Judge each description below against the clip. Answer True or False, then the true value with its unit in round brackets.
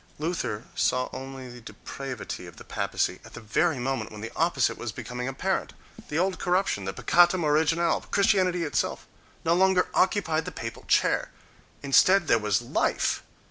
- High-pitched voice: False (150 Hz)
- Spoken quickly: False (165 wpm)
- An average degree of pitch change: False (6.2 semitones)